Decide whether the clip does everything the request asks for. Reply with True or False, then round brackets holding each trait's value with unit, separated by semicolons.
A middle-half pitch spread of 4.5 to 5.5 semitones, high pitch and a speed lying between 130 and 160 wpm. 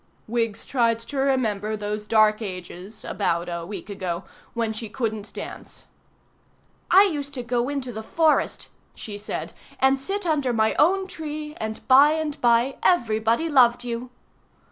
True (4.8 semitones; 235 Hz; 150 wpm)